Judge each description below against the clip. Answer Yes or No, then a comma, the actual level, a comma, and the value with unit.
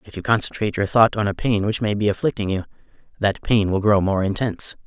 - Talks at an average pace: No, fast, 235 wpm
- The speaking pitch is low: Yes, low, 105 Hz